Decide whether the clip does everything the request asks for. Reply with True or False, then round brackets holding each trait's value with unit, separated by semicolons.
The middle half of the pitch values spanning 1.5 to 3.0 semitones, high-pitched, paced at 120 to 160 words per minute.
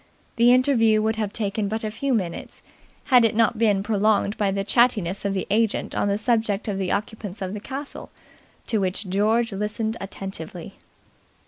False (2.4 semitones; 210 Hz; 180 wpm)